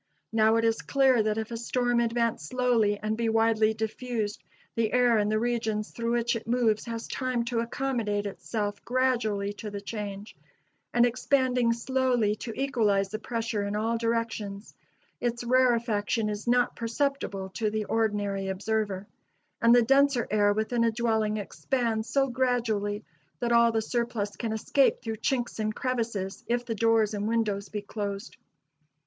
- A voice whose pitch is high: Yes, high, 225 Hz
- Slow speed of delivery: No, average, 160 wpm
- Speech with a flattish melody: Yes, narrow, 2.3 semitones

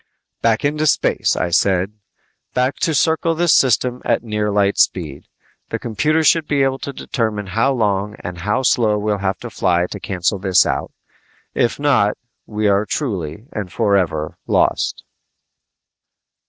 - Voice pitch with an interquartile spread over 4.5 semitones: Yes, average, 5.3 semitones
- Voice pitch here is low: Yes, low, 105 Hz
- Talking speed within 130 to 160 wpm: Yes, average, 155 wpm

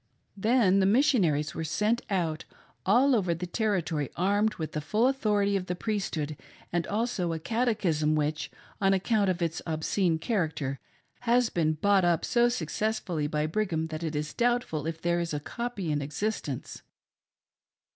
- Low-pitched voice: No, medium, 180 Hz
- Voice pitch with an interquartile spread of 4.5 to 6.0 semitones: Yes, wide, 5.5 semitones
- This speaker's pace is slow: No, average, 160 wpm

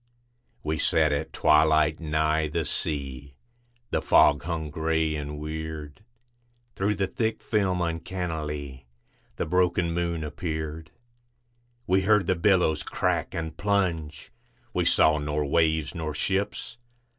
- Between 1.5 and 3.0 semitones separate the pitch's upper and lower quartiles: Yes, average, 2.7 semitones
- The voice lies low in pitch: Yes, very low, 80 Hz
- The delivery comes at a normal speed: No, slow, 120 wpm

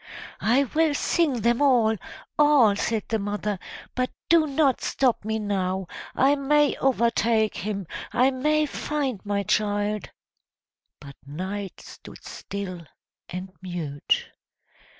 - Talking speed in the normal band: No, slow, 120 wpm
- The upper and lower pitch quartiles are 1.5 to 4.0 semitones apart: No, wide, 5.4 semitones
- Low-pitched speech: No, high, 220 Hz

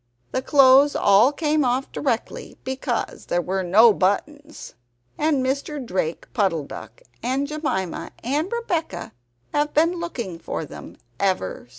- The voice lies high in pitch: Yes, very high, 260 Hz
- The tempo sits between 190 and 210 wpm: No, average, 140 wpm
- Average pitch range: No, wide, 7.3 semitones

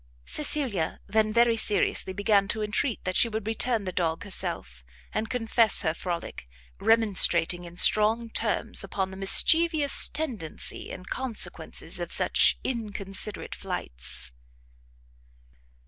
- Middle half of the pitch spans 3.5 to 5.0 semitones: Yes, average, 3.9 semitones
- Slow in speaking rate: Yes, slow, 120 wpm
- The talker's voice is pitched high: Yes, high, 210 Hz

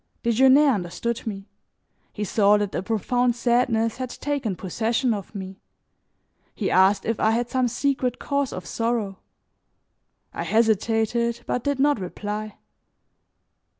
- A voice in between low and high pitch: No, high, 230 Hz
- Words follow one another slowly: Yes, slow, 130 wpm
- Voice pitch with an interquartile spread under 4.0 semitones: Yes, average, 3.2 semitones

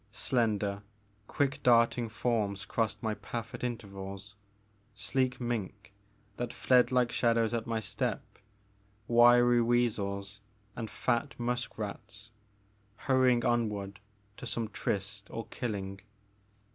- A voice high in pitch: No, low, 115 Hz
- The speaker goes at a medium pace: No, slow, 110 wpm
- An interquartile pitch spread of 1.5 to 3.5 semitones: Yes, average, 2.9 semitones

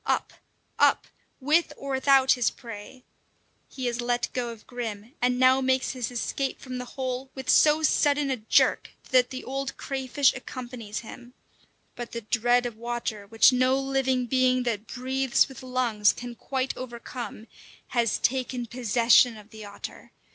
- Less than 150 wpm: No, average, 160 wpm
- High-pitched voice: Yes, very high, 250 Hz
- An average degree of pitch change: No, narrow, 1.9 semitones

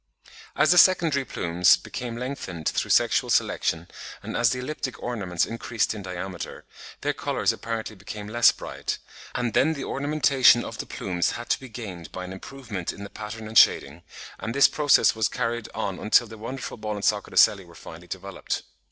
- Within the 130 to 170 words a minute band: No, average, 185 wpm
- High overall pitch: No, low, 110 Hz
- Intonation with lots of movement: No, average, 4.7 semitones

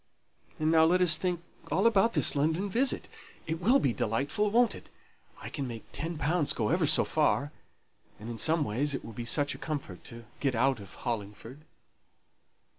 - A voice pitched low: No, medium, 150 Hz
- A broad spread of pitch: Yes, wide, 6.5 semitones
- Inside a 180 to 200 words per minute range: Yes, average, 190 wpm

